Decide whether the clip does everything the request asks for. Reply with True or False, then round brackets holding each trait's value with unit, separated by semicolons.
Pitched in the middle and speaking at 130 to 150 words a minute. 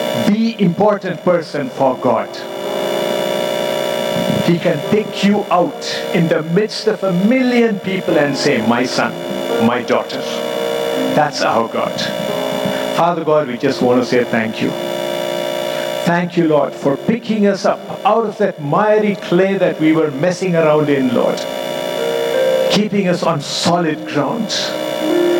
True (155 Hz; 140 wpm)